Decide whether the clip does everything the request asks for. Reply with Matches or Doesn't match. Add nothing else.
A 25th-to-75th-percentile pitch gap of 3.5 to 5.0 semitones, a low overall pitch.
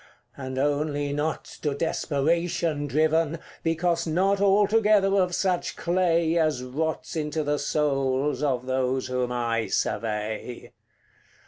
Doesn't match